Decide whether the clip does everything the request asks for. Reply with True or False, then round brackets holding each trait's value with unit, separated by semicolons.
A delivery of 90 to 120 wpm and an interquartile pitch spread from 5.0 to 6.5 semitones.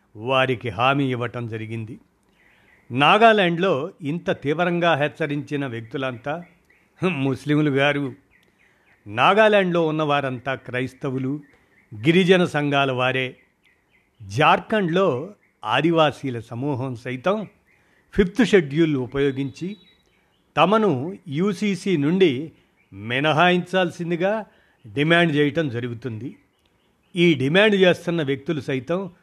False (75 wpm; 5.3 semitones)